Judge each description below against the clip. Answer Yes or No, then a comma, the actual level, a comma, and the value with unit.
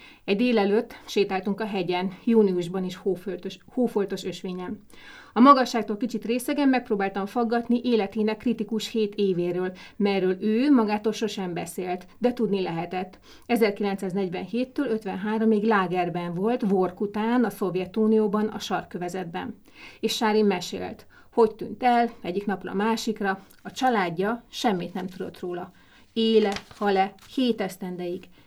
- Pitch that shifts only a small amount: No, average, 3.2 semitones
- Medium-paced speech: Yes, average, 120 wpm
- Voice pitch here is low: No, high, 205 Hz